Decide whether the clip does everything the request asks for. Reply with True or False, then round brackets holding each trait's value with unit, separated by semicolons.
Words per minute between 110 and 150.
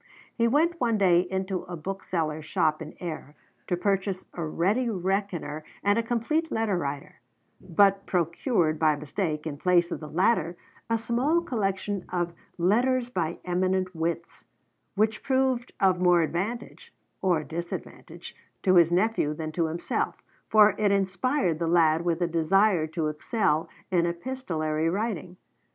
True (145 wpm)